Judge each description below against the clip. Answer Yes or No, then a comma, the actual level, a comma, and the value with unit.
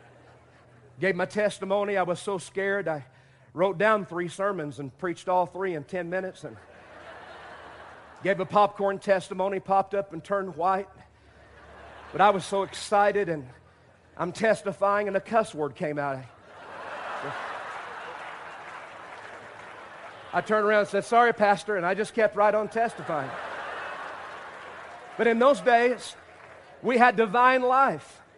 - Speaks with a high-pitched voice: Yes, high, 195 Hz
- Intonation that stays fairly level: No, average, 3.4 semitones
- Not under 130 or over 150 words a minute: Yes, average, 140 wpm